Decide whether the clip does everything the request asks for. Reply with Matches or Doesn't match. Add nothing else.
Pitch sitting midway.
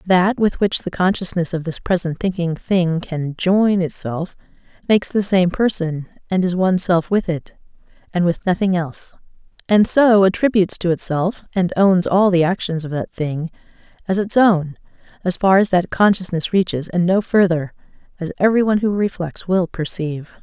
Matches